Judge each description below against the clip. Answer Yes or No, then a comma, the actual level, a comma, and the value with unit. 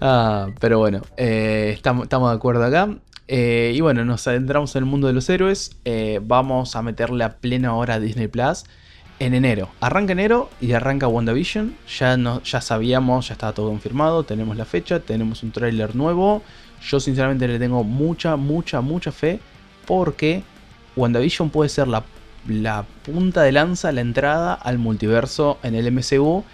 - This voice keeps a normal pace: Yes, average, 170 wpm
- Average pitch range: Yes, average, 4.6 semitones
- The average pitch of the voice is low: Yes, low, 125 Hz